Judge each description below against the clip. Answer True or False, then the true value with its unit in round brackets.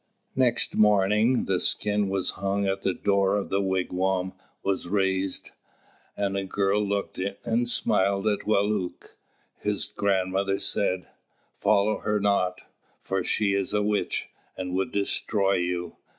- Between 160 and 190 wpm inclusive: False (140 wpm)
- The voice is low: True (100 Hz)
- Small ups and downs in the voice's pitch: True (1.4 semitones)